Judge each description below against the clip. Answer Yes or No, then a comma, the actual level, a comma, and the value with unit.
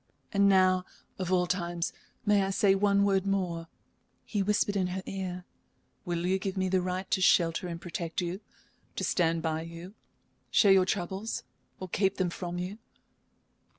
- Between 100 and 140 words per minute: No, average, 170 wpm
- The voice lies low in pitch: No, medium, 185 Hz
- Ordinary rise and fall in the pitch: No, narrow, 1.9 semitones